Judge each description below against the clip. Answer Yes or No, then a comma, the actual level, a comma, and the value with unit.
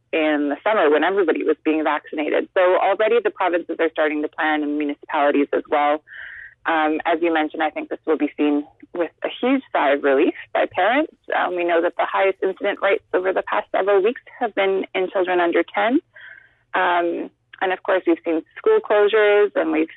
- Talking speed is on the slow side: No, average, 200 wpm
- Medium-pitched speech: Yes, medium, 175 Hz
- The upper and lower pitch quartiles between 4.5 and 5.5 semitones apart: Yes, average, 5.0 semitones